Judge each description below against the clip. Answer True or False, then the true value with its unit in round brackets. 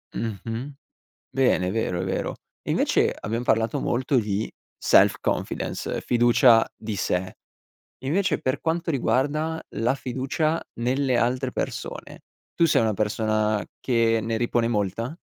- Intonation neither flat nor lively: True (3.4 semitones)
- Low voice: True (120 Hz)